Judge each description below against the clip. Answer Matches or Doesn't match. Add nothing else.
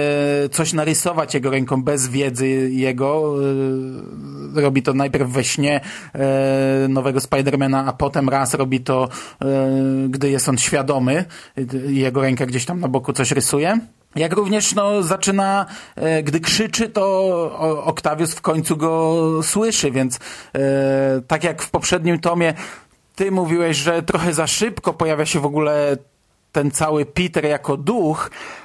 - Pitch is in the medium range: Matches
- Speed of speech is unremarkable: Matches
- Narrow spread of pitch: Doesn't match